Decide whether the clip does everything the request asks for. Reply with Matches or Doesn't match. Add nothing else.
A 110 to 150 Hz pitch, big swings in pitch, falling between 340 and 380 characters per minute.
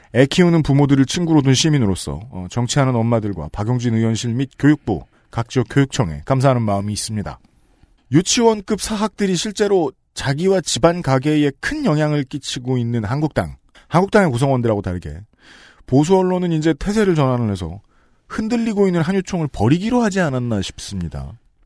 Matches